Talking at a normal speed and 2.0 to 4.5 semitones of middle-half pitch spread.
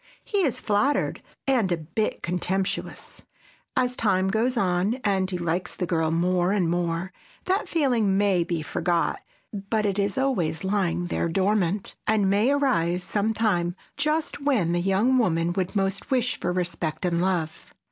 Yes: average, 155 wpm; average, 4.1 semitones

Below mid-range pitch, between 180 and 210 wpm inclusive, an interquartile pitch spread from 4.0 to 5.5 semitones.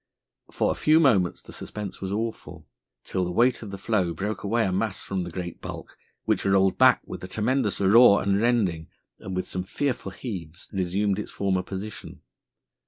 No: low, 100 Hz; average, 185 wpm; average, 3.0 semitones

